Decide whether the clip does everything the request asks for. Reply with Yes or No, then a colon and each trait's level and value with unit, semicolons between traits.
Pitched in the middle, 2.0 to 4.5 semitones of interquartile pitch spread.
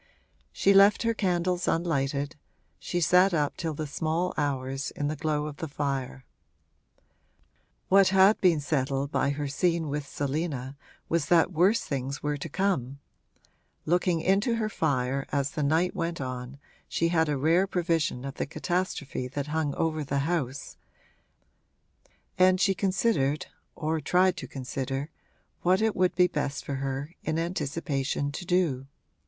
Yes: medium, 155 Hz; average, 4.2 semitones